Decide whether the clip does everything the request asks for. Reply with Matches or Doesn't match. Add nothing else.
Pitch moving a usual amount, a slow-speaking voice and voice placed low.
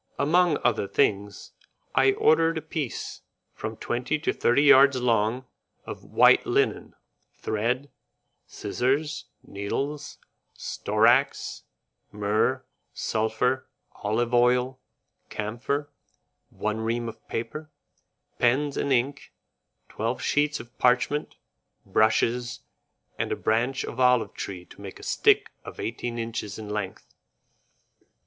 Matches